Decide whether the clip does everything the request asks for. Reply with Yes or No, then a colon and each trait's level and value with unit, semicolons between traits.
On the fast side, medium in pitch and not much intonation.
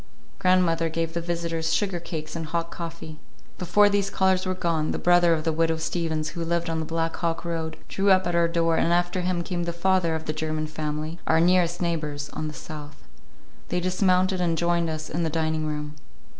Yes: fast, 210 wpm; medium, 165 Hz; narrow, 1.7 semitones